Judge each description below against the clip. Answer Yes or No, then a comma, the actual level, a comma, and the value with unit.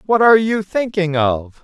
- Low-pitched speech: No, medium, 185 Hz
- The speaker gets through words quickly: No, average, 185 wpm